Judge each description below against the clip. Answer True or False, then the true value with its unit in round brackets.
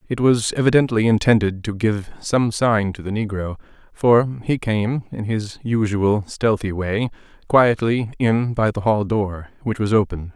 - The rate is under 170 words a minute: True (160 wpm)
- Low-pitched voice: True (110 Hz)